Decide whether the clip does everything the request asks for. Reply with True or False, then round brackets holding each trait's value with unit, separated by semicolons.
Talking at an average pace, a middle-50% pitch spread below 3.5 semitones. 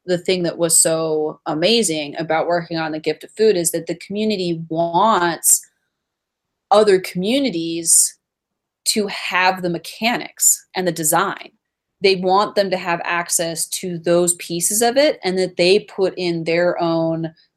True (155 wpm; 2.7 semitones)